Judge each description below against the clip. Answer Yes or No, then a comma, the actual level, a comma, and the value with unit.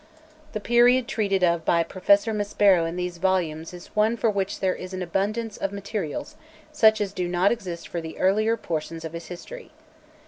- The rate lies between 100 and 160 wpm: No, average, 185 wpm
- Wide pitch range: No, average, 3.7 semitones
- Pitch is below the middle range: No, high, 190 Hz